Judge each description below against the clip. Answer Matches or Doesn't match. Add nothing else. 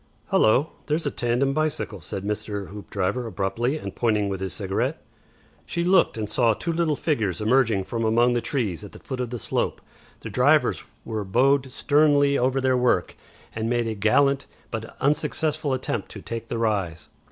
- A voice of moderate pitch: Doesn't match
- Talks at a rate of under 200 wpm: Matches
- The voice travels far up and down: Doesn't match